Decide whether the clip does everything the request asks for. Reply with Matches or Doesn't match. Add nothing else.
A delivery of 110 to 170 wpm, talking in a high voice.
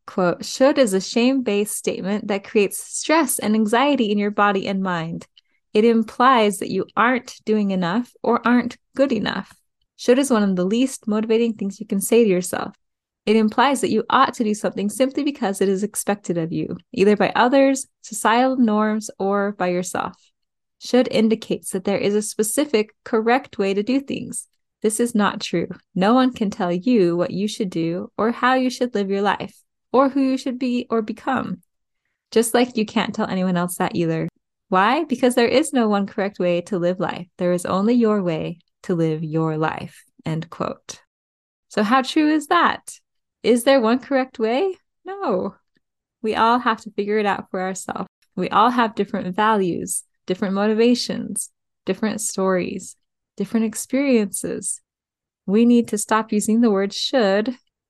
Doesn't match